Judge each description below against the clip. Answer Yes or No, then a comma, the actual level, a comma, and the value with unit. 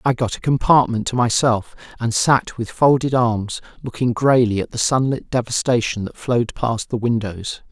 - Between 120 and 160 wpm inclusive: No, average, 170 wpm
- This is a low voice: Yes, low, 120 Hz